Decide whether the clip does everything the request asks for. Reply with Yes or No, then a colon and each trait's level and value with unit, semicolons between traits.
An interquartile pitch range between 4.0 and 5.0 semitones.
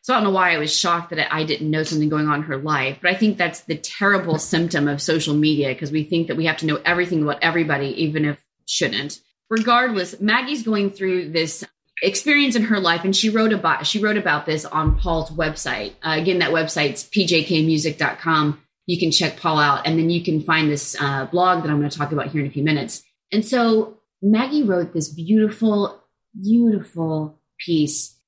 Yes: average, 4.6 semitones